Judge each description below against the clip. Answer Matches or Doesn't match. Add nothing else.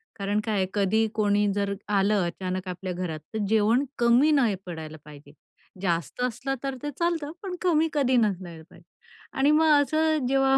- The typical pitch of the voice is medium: Doesn't match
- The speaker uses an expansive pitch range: Matches